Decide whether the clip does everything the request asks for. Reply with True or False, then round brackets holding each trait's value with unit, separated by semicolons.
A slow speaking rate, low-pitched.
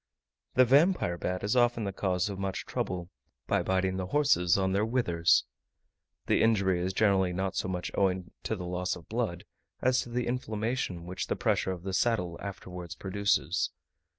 False (180 wpm; 95 Hz)